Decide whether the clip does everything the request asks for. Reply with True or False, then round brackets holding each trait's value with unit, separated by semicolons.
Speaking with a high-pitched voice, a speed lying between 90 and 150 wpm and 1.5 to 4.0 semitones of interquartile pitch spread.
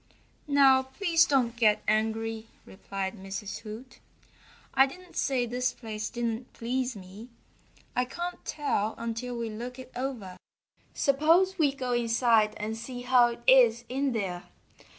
True (240 Hz; 140 wpm; 3.1 semitones)